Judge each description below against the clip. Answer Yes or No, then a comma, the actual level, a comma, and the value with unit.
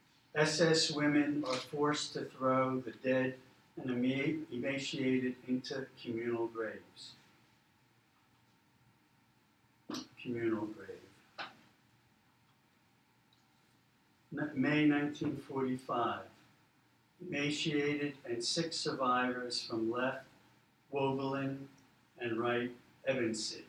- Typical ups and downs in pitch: Yes, average, 3.2 semitones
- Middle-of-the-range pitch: No, low, 130 Hz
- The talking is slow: Yes, slow, 70 wpm